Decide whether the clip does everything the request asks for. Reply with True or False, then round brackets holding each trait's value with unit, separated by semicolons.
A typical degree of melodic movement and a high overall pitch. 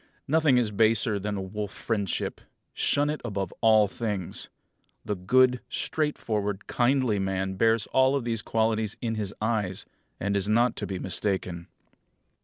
False (3.3 semitones; 110 Hz)